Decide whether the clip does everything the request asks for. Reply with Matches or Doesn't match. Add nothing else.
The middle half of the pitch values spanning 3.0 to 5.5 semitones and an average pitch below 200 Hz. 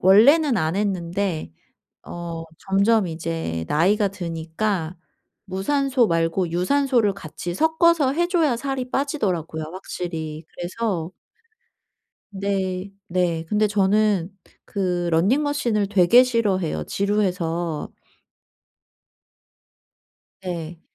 Matches